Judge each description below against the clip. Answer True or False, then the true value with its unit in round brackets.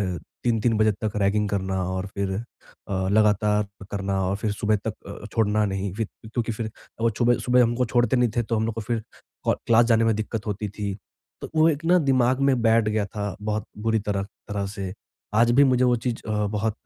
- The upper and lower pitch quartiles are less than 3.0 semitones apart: True (2.5 semitones)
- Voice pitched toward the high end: False (110 Hz)